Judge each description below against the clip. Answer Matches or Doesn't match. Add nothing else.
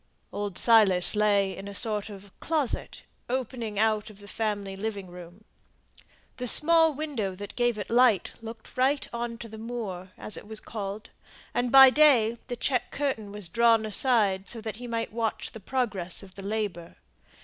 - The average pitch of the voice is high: Matches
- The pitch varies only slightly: Doesn't match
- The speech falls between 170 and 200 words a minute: Matches